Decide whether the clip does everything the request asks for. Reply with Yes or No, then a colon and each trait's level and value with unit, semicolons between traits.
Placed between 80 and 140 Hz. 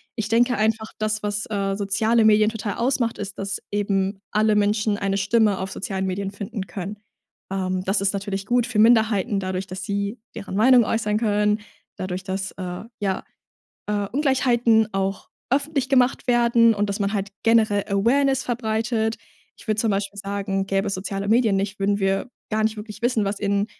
No: high, 210 Hz